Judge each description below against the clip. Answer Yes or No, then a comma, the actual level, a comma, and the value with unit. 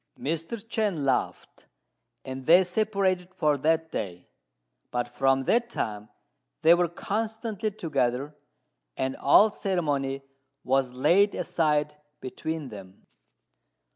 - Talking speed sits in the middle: No, slow, 110 wpm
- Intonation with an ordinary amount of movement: No, wide, 6.1 semitones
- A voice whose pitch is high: No, medium, 155 Hz